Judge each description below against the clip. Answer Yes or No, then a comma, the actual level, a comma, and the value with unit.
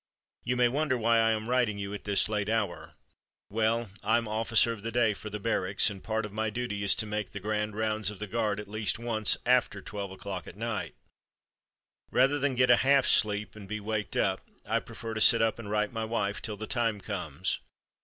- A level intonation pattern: Yes, narrow, 2.0 semitones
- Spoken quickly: Yes, fast, 225 wpm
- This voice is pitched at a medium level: No, low, 110 Hz